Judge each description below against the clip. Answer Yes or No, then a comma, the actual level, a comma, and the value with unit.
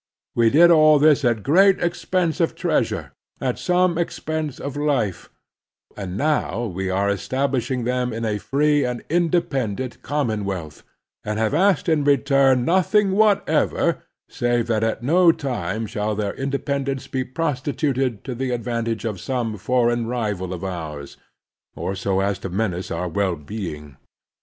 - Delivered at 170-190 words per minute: No, average, 150 wpm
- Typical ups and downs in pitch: No, wide, 6.0 semitones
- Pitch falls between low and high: No, low, 125 Hz